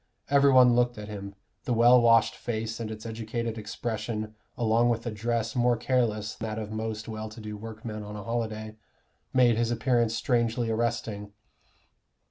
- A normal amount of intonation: No, narrow, 1.6 semitones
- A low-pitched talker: Yes, low, 115 Hz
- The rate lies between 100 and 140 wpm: No, average, 170 wpm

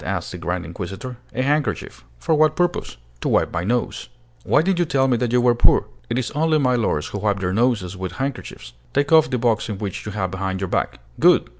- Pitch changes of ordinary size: No, wide, 6.2 semitones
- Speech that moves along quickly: Yes, fast, 220 wpm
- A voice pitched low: Yes, low, 120 Hz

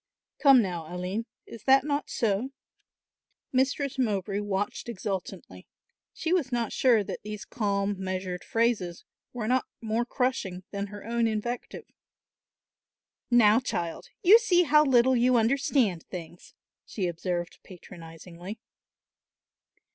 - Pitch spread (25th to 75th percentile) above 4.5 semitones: Yes, average, 5.2 semitones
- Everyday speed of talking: No, slow, 120 wpm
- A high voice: Yes, high, 220 Hz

